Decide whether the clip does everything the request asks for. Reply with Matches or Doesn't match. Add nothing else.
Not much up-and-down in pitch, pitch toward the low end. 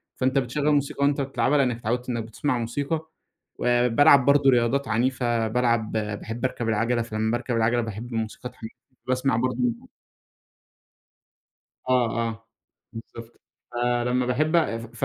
Matches